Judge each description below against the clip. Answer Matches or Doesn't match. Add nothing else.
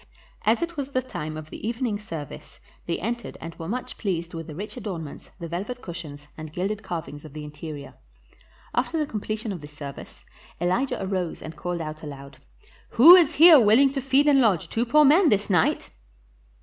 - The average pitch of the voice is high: Matches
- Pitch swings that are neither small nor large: Doesn't match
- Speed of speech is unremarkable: Matches